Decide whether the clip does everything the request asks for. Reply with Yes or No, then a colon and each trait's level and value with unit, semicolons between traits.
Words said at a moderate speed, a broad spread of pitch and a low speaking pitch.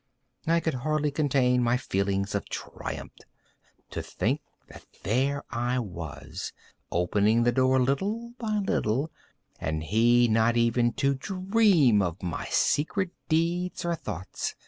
No: slow, 130 wpm; wide, 6.9 semitones; low, 125 Hz